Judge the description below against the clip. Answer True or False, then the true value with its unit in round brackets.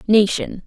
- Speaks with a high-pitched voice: True (205 Hz)